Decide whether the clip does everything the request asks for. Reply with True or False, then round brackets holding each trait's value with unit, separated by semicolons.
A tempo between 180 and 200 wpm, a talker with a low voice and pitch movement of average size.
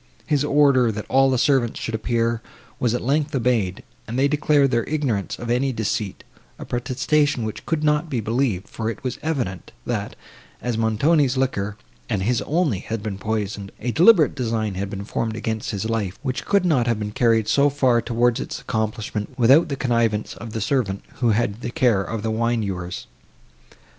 True (185 wpm; 115 Hz; 3.9 semitones)